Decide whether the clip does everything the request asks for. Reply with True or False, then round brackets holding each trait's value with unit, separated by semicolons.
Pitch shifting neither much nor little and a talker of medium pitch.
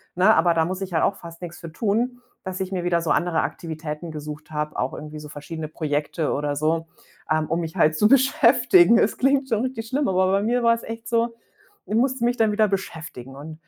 False (6.5 semitones; 180 Hz)